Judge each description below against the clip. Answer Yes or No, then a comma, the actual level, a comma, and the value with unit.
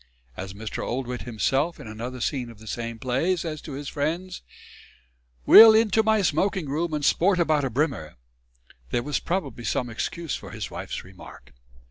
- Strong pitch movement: Yes, wide, 6.2 semitones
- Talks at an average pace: Yes, average, 170 wpm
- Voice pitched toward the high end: No, medium, 140 Hz